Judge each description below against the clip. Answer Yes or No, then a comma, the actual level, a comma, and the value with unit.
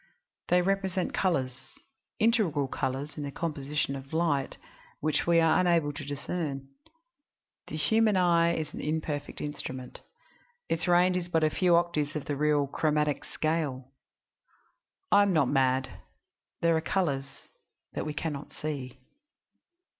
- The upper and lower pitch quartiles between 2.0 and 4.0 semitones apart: Yes, average, 3.5 semitones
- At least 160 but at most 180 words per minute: No, average, 140 wpm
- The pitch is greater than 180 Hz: No, medium, 155 Hz